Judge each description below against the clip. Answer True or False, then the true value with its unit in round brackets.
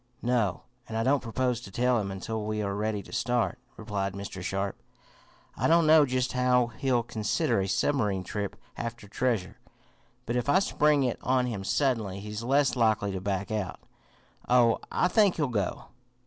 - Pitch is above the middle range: False (115 Hz)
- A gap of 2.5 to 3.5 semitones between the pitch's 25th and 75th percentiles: False (4.0 semitones)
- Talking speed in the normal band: True (175 wpm)